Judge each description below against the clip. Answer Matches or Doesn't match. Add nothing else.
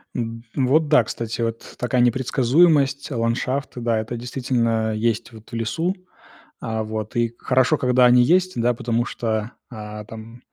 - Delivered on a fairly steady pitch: Matches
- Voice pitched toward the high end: Doesn't match